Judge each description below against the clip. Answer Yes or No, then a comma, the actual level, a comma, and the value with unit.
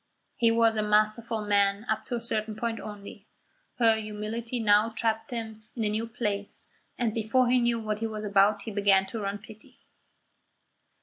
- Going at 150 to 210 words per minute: Yes, average, 180 wpm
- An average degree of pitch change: No, narrow, 1.6 semitones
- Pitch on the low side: No, high, 220 Hz